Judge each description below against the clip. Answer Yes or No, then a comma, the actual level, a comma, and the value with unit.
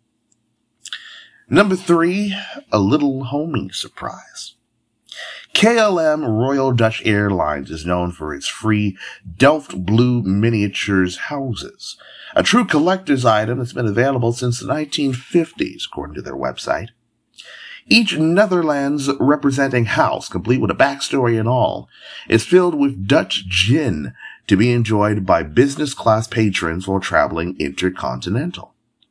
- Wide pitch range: Yes, wide, 8.3 semitones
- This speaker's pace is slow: Yes, slow, 120 wpm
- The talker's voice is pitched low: Yes, low, 125 Hz